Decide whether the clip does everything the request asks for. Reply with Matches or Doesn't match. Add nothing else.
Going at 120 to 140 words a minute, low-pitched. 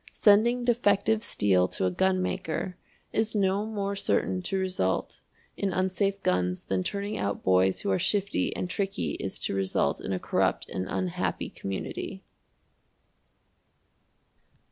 Doesn't match